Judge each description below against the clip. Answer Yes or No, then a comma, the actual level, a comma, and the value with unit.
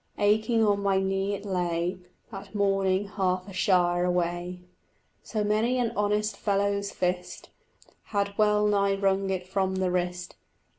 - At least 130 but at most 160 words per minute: Yes, average, 145 wpm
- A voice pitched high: Yes, high, 195 Hz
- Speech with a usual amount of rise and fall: No, narrow, 2.0 semitones